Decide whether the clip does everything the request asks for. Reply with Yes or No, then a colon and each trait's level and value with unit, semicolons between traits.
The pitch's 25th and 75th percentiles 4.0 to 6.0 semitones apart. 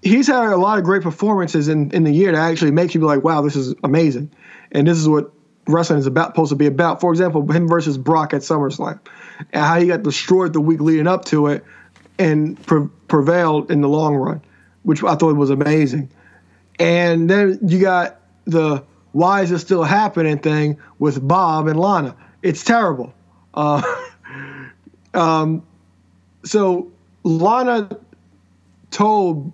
No: average, 3.3 semitones